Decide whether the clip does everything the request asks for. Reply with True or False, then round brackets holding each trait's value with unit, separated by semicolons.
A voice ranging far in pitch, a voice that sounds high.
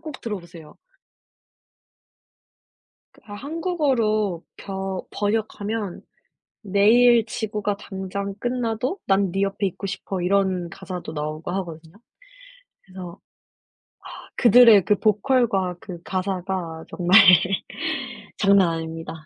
False (3.2 semitones; 195 Hz)